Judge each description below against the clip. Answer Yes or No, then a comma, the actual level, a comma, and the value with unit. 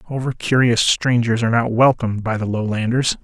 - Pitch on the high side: No, low, 115 Hz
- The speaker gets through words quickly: No, average, 165 wpm